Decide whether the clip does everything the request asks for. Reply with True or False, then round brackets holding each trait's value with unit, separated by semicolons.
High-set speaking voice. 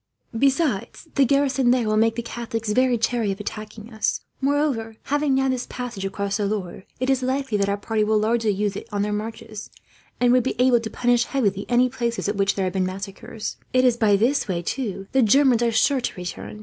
True (225 Hz)